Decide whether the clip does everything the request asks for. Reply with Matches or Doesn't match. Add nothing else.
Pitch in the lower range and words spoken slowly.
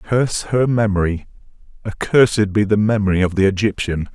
Matches